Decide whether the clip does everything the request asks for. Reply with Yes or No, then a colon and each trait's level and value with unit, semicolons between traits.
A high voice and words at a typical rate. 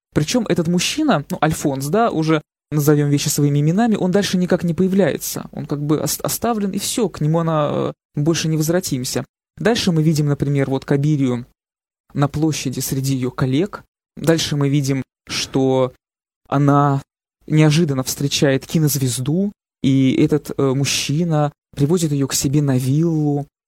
No: medium, 150 Hz; average, 140 wpm